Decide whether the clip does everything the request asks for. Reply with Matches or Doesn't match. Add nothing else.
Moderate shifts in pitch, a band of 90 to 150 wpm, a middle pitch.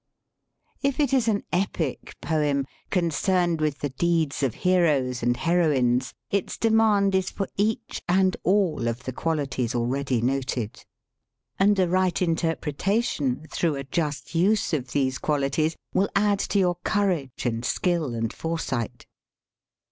Doesn't match